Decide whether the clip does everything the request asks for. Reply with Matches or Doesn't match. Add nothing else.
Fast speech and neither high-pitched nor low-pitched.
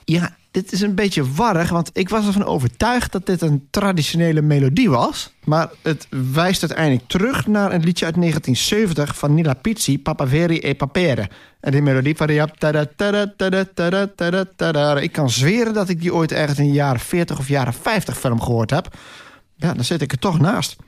Doesn't match